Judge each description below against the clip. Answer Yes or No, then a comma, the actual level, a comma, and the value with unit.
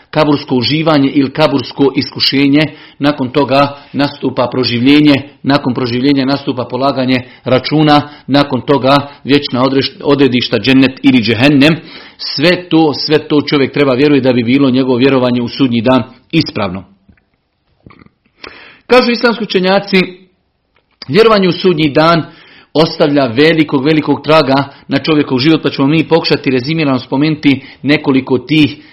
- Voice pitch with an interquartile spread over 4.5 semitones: No, average, 2.8 semitones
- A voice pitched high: No, medium, 140 Hz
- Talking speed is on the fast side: No, average, 120 wpm